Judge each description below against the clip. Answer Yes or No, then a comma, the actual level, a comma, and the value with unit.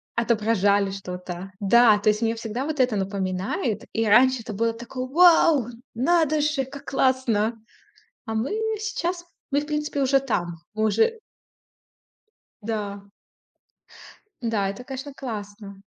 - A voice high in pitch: Yes, high, 230 Hz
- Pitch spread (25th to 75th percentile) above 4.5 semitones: Yes, average, 4.9 semitones